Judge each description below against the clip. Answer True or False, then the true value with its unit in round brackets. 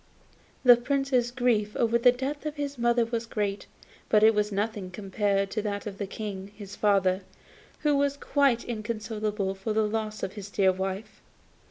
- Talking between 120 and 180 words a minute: True (175 wpm)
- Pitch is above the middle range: True (215 Hz)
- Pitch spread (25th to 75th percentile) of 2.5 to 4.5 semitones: True (3.1 semitones)